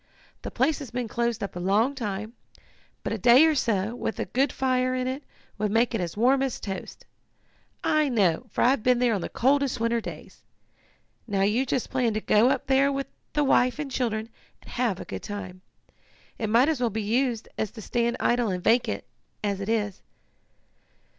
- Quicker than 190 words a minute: Yes, average, 200 wpm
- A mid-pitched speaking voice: No, high, 235 Hz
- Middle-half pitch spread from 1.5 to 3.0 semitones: No, average, 3.5 semitones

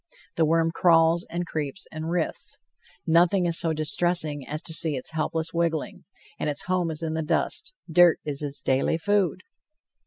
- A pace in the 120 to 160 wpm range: No, average, 175 wpm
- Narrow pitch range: Yes, narrow, 1.9 semitones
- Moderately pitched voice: Yes, medium, 165 Hz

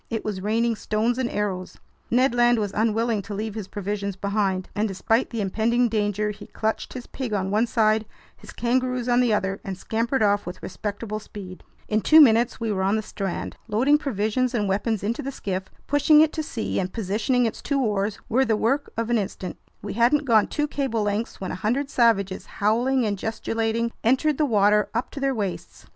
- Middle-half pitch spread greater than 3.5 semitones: No, average, 2.9 semitones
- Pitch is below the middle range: No, high, 220 Hz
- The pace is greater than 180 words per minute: Yes, fast, 205 wpm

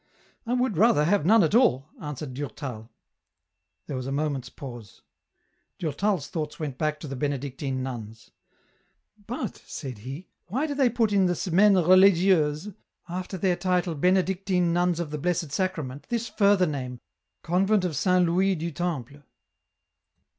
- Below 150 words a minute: No, average, 170 wpm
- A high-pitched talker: No, medium, 170 Hz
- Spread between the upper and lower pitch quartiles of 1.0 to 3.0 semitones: No, average, 5.2 semitones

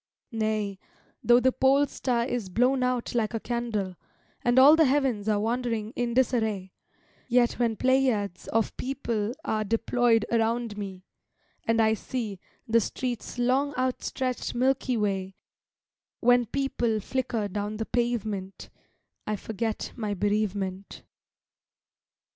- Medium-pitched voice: No, high, 230 Hz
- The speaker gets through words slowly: Yes, slow, 125 wpm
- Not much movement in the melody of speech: No, average, 3.1 semitones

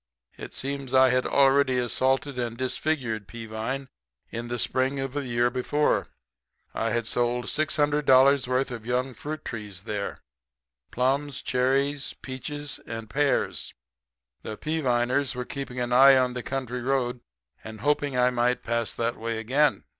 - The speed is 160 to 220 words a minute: No, average, 145 wpm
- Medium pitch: No, low, 125 Hz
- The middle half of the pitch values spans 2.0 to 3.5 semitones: Yes, narrow, 2.5 semitones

